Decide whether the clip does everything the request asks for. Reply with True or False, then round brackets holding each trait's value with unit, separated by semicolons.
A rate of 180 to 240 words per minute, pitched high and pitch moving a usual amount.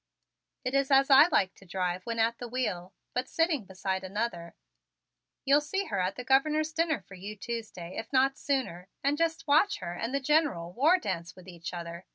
False (200 wpm; 230 Hz; 7.3 semitones)